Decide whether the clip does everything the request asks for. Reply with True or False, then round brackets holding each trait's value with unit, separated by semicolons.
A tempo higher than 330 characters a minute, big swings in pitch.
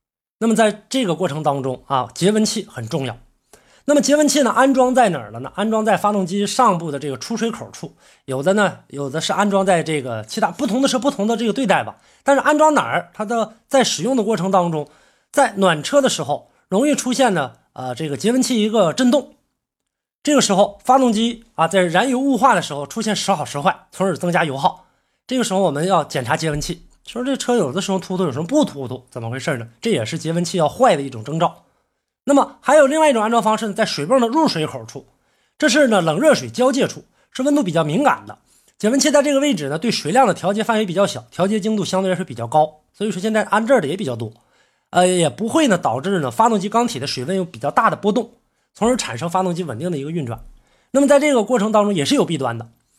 True (355 characters per minute; 8.0 semitones)